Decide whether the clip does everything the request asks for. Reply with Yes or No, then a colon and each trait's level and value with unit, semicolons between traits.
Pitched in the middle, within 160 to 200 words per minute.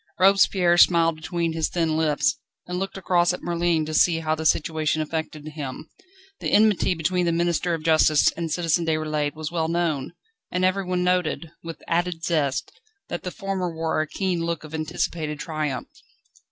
Yes: medium, 165 Hz; average, 170 wpm